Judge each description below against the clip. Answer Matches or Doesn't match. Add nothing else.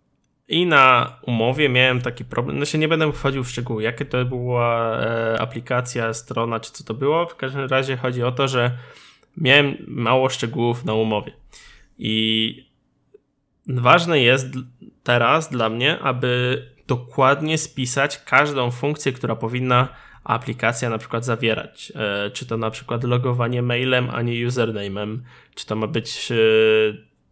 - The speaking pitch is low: Matches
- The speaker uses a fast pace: Doesn't match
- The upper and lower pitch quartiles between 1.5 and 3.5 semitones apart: Matches